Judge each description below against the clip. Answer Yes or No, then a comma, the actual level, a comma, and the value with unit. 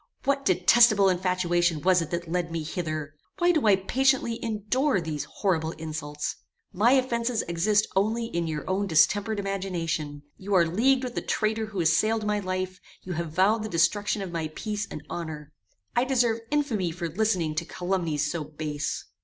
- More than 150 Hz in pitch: Yes, medium, 185 Hz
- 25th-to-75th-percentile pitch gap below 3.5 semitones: No, average, 4.8 semitones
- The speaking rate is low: No, average, 170 wpm